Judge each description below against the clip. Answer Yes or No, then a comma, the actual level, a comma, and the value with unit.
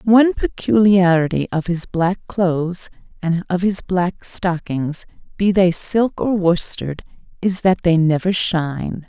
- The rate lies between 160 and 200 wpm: No, average, 140 wpm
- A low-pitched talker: No, medium, 180 Hz